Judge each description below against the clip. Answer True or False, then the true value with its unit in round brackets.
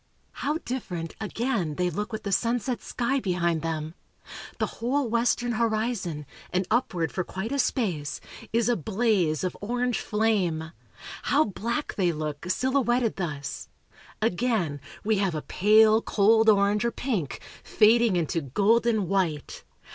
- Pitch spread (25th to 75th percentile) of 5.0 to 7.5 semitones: True (5.4 semitones)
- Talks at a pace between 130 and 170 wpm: True (140 wpm)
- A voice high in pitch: True (210 Hz)